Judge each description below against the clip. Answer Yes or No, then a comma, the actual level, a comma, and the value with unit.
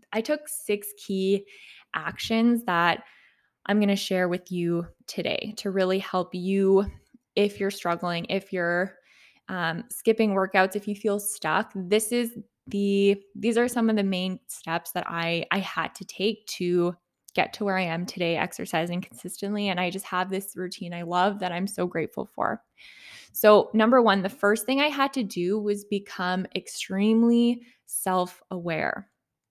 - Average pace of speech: Yes, average, 165 wpm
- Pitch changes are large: No, average, 2.8 semitones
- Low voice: No, high, 195 Hz